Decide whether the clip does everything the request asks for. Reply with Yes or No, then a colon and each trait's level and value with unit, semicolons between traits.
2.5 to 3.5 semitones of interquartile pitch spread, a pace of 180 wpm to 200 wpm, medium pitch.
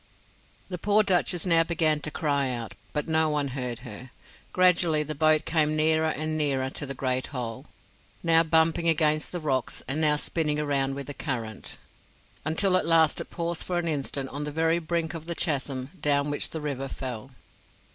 Yes: average, 3.0 semitones; average, 185 wpm; medium, 155 Hz